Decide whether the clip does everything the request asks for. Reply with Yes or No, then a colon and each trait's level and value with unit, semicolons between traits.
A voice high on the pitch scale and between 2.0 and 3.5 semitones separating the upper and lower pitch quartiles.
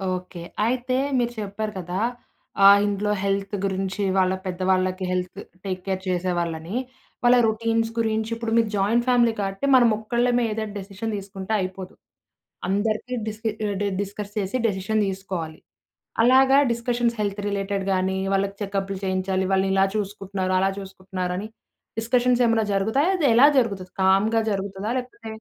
Yes: high, 200 Hz; average, 3.1 semitones